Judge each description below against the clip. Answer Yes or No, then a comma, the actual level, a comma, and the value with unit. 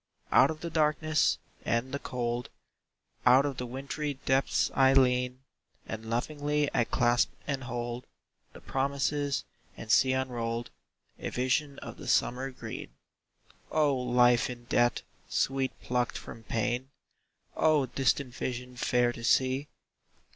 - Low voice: Yes, low, 130 Hz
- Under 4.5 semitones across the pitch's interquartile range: Yes, narrow, 2.4 semitones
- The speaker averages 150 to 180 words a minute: No, slow, 135 wpm